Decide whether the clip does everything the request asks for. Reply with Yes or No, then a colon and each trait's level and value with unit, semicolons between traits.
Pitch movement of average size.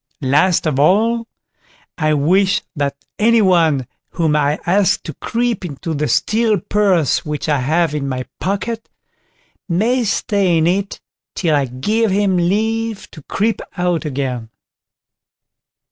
No: wide, 5.7 semitones